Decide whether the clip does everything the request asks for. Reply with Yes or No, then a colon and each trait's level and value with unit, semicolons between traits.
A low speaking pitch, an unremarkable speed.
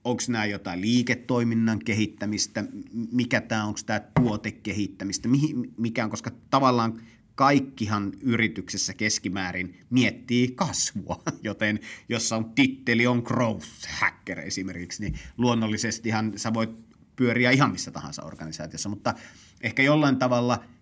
Yes: low, 115 Hz; average, 120 wpm